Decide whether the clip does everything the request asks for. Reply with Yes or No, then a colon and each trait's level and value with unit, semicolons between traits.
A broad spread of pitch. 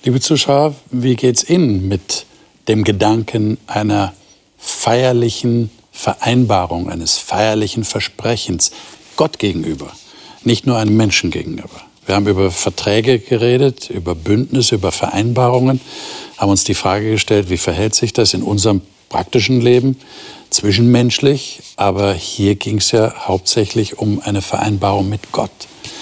No: average, 3.5 semitones